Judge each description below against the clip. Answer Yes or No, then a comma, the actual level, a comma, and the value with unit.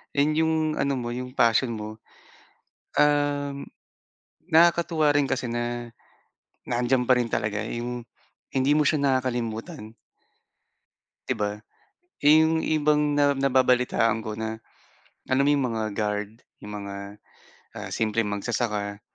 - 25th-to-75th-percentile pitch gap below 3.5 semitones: No, average, 4.5 semitones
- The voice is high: No, low, 125 Hz